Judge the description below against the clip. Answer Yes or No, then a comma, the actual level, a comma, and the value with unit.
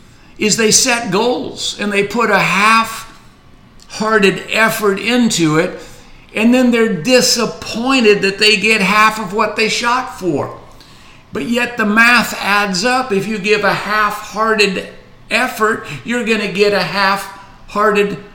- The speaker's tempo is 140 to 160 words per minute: Yes, average, 150 wpm